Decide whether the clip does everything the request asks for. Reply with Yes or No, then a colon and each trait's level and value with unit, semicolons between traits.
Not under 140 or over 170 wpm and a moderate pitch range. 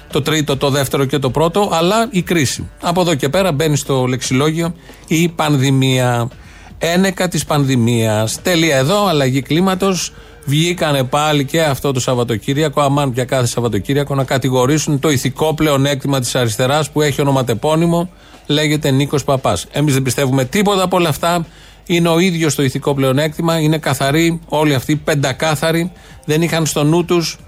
Yes: average, 155 wpm; average, 3.4 semitones